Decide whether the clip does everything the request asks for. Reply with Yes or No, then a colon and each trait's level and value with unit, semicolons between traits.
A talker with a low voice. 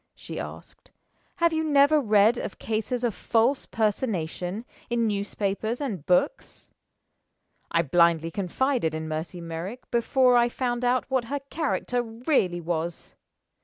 No: high, 225 Hz